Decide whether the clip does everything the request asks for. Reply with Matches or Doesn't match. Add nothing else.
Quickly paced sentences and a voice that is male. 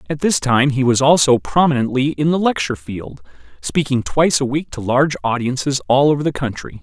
Doesn't match